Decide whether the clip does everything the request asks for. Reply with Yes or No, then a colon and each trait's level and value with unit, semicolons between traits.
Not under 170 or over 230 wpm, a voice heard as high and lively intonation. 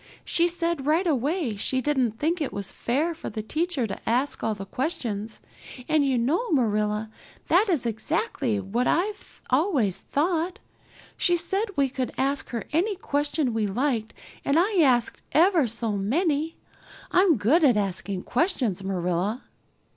No: average, 155 wpm; very high, 270 Hz; wide, 7.2 semitones